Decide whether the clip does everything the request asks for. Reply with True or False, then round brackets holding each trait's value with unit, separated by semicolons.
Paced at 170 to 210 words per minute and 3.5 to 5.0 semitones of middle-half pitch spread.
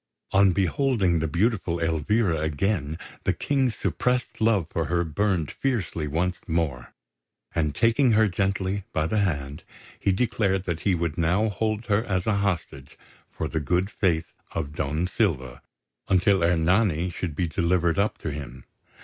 False (155 wpm; 4.2 semitones)